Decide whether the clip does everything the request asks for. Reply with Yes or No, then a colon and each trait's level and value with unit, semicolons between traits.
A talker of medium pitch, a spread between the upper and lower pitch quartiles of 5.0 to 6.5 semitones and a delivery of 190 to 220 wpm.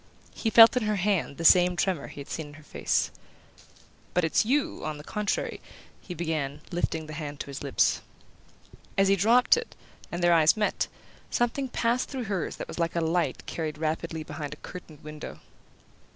Yes: medium, 170 Hz; average, 5.3 semitones; average, 195 wpm